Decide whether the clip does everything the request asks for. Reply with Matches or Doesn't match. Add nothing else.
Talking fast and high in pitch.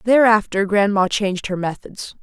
Doesn't match